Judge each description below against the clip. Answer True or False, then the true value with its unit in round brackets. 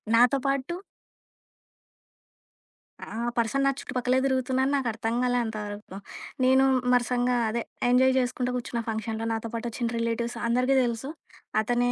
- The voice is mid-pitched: False (245 Hz)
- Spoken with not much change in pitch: True (2.1 semitones)